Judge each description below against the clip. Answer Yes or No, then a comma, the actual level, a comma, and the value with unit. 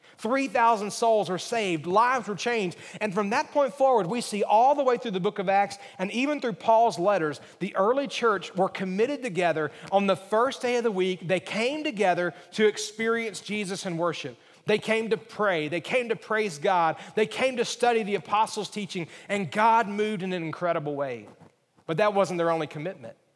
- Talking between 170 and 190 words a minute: No, average, 200 wpm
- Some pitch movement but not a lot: Yes, average, 4.1 semitones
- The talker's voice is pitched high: Yes, high, 210 Hz